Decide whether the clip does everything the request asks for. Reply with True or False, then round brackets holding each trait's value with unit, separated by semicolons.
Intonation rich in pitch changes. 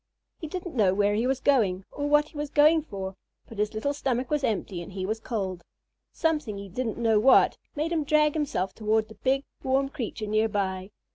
True (6.0 semitones)